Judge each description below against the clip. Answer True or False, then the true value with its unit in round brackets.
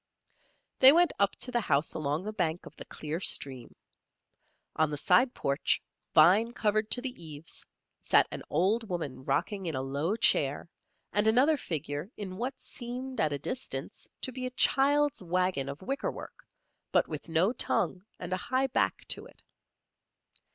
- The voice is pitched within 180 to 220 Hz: True (185 Hz)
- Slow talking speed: False (165 wpm)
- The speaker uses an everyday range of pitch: False (8.0 semitones)